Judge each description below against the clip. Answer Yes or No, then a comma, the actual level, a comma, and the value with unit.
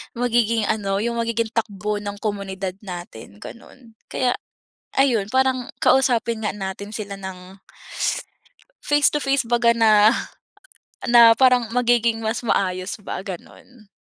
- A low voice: No, high, 225 Hz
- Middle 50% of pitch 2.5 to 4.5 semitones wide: Yes, average, 3.3 semitones